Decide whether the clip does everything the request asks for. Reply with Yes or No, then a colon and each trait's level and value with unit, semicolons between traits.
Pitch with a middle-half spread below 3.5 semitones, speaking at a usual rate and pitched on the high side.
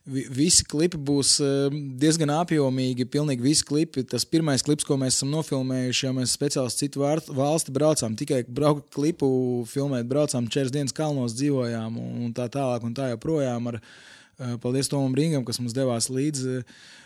No: average, 2.7 semitones; average, 150 wpm; low, 135 Hz